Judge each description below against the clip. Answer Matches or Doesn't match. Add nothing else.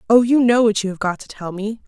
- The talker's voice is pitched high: Matches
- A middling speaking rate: Doesn't match